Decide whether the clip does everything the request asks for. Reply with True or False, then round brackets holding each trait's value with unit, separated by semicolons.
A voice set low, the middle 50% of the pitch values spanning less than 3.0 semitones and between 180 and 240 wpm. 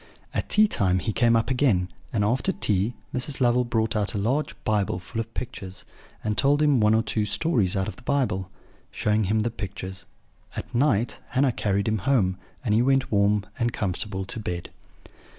False (110 Hz; 4.0 semitones; 190 wpm)